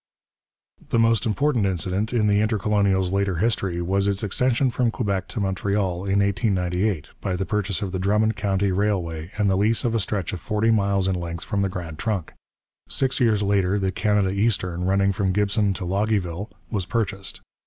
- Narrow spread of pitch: Yes, narrow, 2.2 semitones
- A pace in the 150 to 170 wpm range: No, average, 185 wpm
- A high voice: No, low, 100 Hz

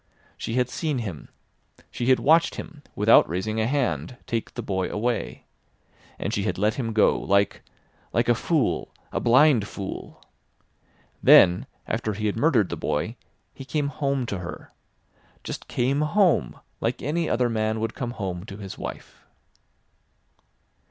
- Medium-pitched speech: No, low, 115 Hz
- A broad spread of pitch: No, average, 4.7 semitones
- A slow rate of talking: No, average, 150 wpm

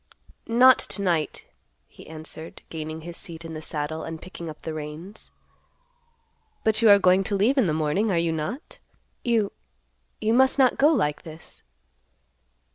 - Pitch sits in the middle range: Yes, medium, 170 Hz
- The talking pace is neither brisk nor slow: Yes, average, 160 wpm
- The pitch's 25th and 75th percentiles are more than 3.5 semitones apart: Yes, wide, 5.5 semitones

